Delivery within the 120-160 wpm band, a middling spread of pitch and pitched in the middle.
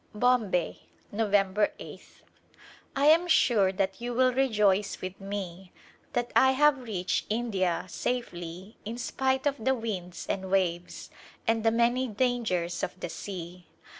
No: average, 145 wpm; average, 4.7 semitones; high, 210 Hz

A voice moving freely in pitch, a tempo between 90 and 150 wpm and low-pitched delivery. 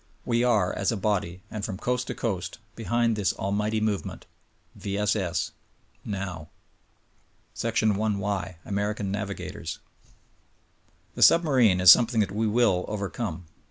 No: narrow, 2.6 semitones; average, 140 wpm; low, 105 Hz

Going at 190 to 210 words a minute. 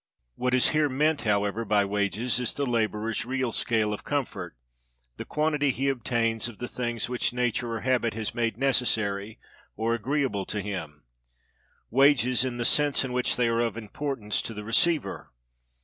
No: average, 170 wpm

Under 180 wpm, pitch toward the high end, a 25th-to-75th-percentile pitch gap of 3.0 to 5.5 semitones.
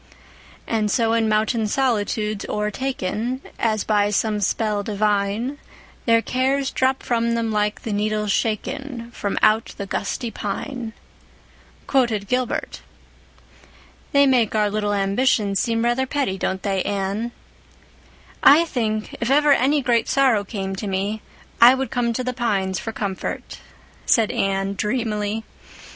Yes: slow, 135 wpm; high, 220 Hz; average, 3.3 semitones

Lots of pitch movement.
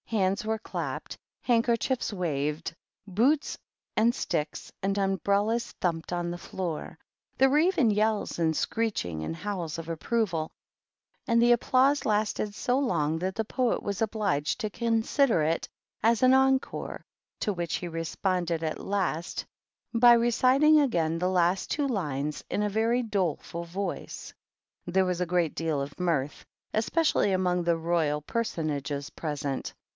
Yes: wide, 5.8 semitones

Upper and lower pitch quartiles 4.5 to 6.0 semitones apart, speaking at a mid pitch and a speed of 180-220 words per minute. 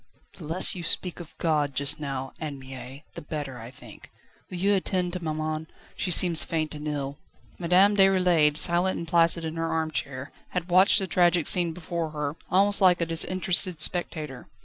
No: average, 3.2 semitones; medium, 165 Hz; average, 185 wpm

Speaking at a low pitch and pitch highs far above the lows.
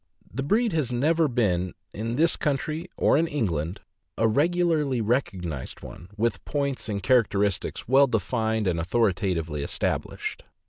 Yes: low, 115 Hz; wide, 6.7 semitones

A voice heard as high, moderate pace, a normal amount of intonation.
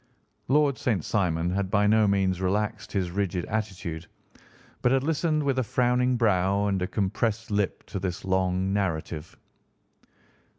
No: low, 100 Hz; average, 145 wpm; average, 3.7 semitones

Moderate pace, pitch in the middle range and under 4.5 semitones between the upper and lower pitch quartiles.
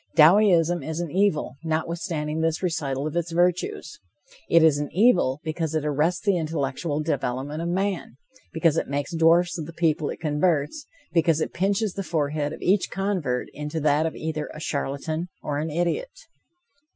Yes: average, 170 wpm; medium, 160 Hz; average, 2.7 semitones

